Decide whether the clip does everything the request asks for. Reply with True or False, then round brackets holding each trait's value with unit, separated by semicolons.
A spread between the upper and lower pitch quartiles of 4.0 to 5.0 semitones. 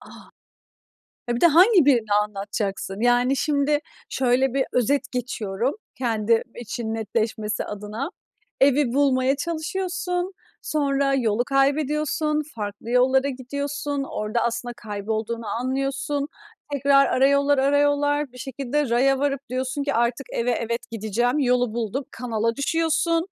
False (3.5 semitones)